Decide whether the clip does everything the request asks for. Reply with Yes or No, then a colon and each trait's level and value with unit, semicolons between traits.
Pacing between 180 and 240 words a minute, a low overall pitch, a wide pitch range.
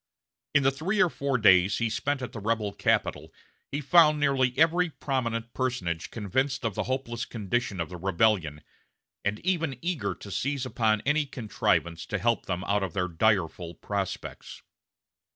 No: average, 165 wpm; low, 115 Hz; wide, 5.8 semitones